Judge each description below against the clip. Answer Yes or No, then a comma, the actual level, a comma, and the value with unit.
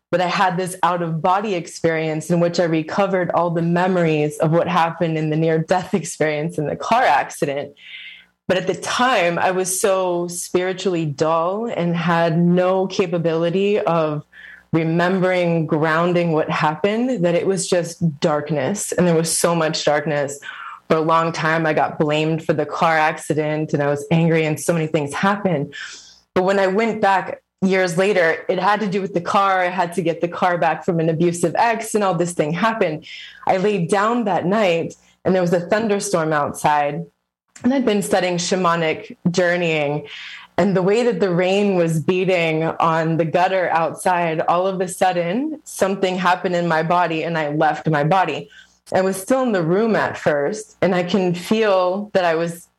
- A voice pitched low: No, medium, 175 Hz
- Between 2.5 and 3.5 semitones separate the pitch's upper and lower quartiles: Yes, average, 2.8 semitones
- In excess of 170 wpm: Yes, average, 185 wpm